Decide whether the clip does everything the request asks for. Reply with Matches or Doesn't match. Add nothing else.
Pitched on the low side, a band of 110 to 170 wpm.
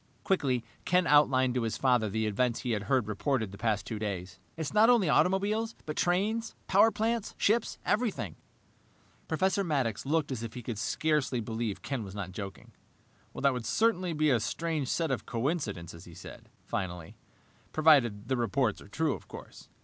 Doesn't match